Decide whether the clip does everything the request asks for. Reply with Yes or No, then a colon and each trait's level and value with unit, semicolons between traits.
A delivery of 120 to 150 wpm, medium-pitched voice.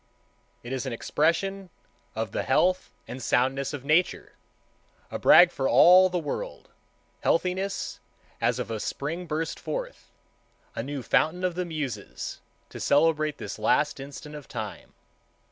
Yes: average, 140 wpm; medium, 155 Hz